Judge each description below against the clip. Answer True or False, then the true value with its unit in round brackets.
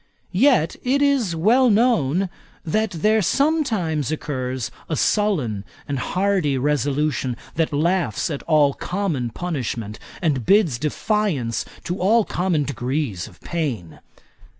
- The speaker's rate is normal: False (120 wpm)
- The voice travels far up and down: True (7.1 semitones)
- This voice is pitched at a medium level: True (160 Hz)